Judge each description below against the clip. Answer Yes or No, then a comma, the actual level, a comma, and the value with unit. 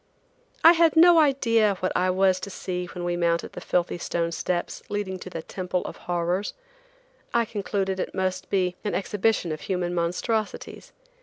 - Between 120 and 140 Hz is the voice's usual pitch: No, medium, 185 Hz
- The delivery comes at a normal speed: Yes, average, 170 wpm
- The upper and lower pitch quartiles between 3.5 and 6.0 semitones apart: No, average, 2.8 semitones